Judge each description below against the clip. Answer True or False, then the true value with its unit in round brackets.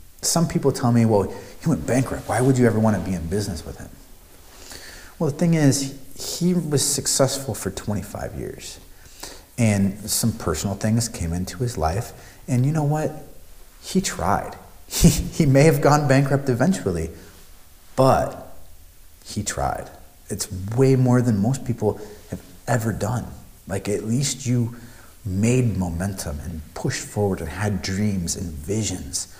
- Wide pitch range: True (5.9 semitones)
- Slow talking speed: False (155 wpm)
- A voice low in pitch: True (105 Hz)